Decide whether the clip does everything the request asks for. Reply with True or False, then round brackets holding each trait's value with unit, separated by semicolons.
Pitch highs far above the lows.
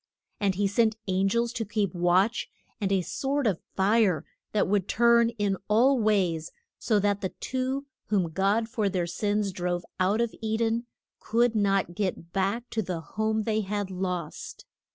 False (3.1 semitones)